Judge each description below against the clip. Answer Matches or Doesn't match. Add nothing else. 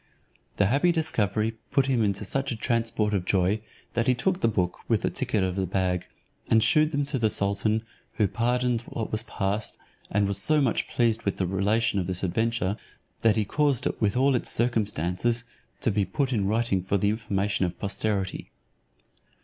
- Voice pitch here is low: Matches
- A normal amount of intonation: Matches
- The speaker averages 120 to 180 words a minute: Doesn't match